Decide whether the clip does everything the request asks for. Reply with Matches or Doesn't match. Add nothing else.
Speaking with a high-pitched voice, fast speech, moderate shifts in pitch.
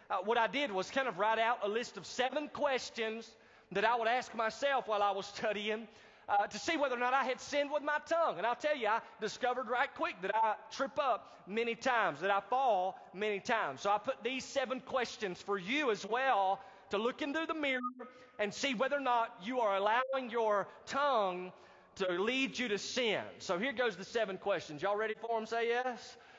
Matches